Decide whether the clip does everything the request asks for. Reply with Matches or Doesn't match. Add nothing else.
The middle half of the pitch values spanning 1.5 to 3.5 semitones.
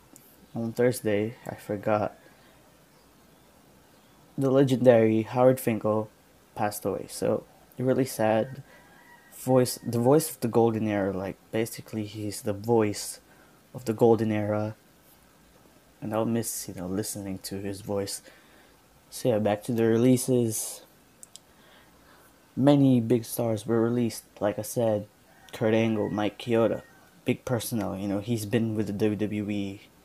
Matches